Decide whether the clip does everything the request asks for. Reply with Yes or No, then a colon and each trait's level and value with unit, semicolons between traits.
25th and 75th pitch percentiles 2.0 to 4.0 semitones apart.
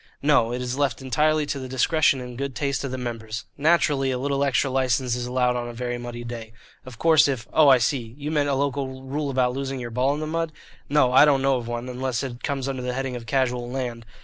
Yes: narrow, 2.4 semitones